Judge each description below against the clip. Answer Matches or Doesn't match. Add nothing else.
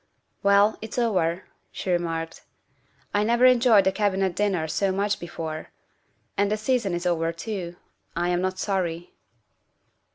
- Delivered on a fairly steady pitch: Doesn't match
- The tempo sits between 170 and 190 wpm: Doesn't match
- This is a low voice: Doesn't match